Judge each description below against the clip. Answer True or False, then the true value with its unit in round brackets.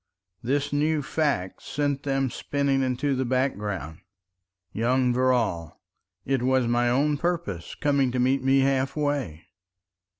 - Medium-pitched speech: False (130 Hz)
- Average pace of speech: False (130 wpm)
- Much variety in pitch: False (2.7 semitones)